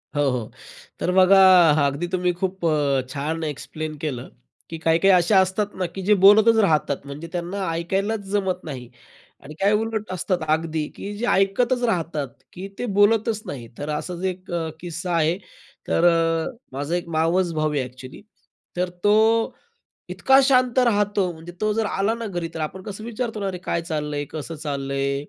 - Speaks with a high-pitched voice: No, medium, 175 Hz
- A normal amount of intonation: Yes, average, 4.8 semitones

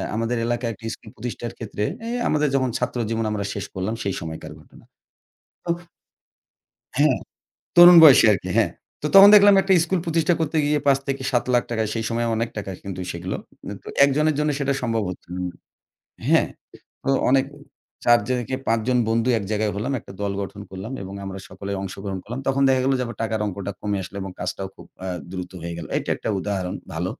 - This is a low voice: Yes, low, 115 Hz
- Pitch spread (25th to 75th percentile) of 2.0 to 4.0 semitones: No, average, 5.3 semitones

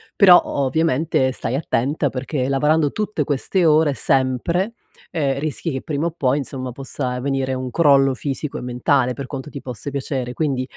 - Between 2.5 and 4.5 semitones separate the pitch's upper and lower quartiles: Yes, average, 2.9 semitones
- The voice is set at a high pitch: No, medium, 140 Hz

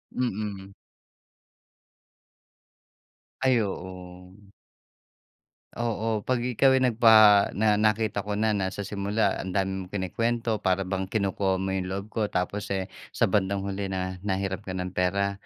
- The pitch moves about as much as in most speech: No, narrow, 2.3 semitones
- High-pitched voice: No, low, 100 Hz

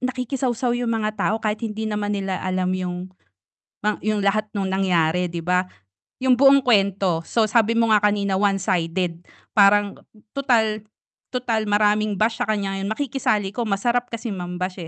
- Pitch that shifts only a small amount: No, average, 3.2 semitones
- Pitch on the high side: Yes, high, 205 Hz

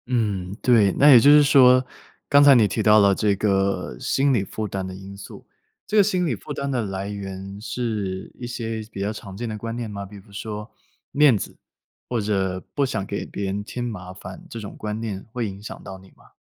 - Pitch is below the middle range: Yes, low, 105 Hz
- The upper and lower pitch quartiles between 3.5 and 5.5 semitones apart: Yes, average, 3.8 semitones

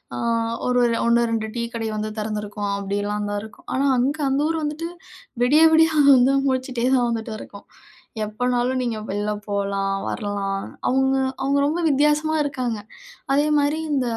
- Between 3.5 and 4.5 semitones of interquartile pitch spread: No, average, 4.9 semitones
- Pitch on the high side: Yes, high, 245 Hz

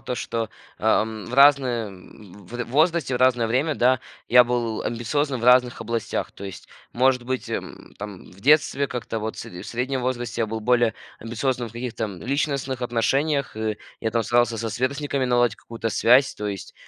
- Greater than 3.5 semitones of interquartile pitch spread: No, narrow, 2.6 semitones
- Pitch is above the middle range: No, low, 120 Hz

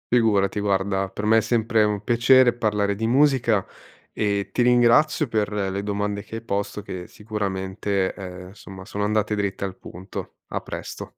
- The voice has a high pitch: No, low, 105 Hz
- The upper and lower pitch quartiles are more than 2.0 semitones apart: Yes, narrow, 2.4 semitones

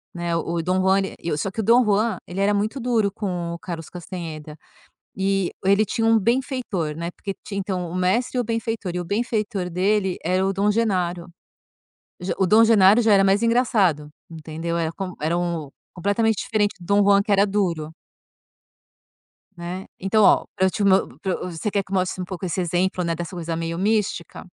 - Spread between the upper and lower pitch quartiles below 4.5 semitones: Yes, average, 3.3 semitones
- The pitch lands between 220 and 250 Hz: No, high, 190 Hz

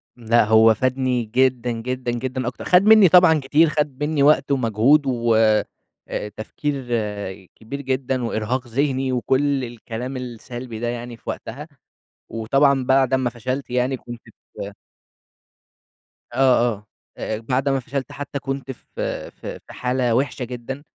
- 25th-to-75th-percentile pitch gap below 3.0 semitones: Yes, narrow, 2.5 semitones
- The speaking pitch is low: Yes, low, 130 Hz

